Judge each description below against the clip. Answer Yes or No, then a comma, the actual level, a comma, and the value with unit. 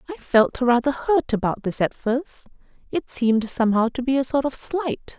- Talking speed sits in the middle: Yes, average, 195 wpm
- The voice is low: No, very high, 255 Hz